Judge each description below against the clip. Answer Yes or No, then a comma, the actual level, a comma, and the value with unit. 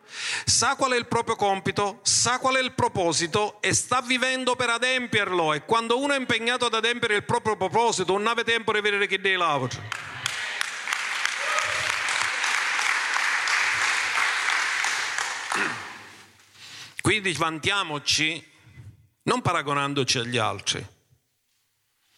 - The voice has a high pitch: Yes, high, 205 Hz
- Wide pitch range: Yes, wide, 7.7 semitones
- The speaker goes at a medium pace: No, slow, 110 wpm